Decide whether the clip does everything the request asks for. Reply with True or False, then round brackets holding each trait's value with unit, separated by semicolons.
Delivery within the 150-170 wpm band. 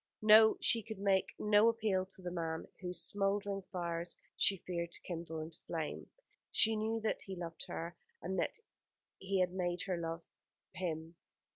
True (165 wpm)